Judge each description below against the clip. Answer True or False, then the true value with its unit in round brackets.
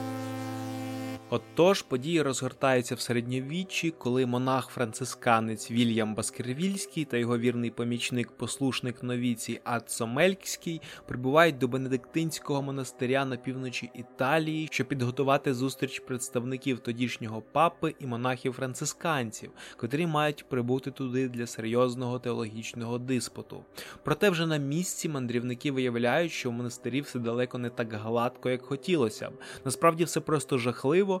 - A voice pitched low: True (130 Hz)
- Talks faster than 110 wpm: True (120 wpm)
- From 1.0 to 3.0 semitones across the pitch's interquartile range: True (2.6 semitones)